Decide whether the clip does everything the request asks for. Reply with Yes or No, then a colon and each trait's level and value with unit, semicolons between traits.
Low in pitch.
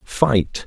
Yes: low, 120 Hz